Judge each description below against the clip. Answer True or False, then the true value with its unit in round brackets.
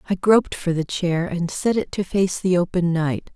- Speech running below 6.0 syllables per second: True (4.8 syllables/s)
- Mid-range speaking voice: True (180 Hz)